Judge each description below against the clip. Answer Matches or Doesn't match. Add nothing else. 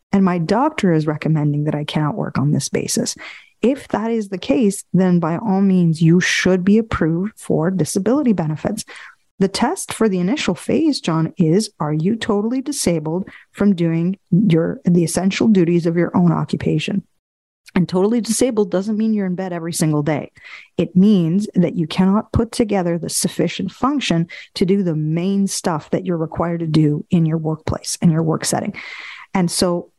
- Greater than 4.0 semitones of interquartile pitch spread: Doesn't match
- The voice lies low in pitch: Doesn't match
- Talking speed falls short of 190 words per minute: Matches